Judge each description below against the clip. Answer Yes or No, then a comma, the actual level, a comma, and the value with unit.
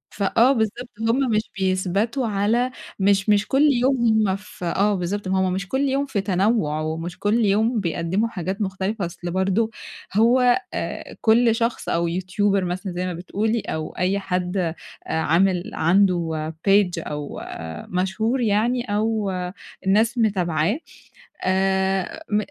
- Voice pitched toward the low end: No, high, 195 Hz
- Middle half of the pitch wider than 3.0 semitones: Yes, average, 3.7 semitones